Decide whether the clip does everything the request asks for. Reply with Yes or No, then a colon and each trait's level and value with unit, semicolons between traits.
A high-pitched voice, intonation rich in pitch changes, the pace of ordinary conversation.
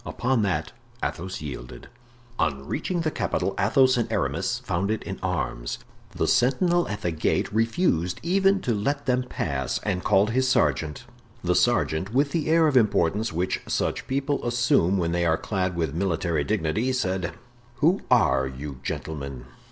No: low, 100 Hz; wide, 7.9 semitones; average, 160 wpm